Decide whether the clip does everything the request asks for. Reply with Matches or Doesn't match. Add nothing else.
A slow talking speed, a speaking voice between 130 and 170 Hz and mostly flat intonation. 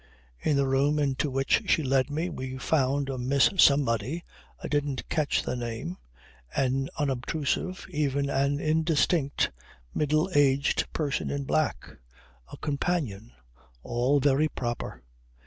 Matches